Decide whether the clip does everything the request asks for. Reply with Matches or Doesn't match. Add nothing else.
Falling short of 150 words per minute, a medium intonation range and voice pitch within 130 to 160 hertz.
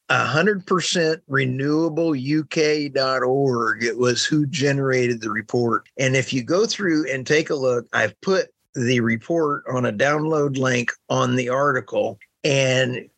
Matches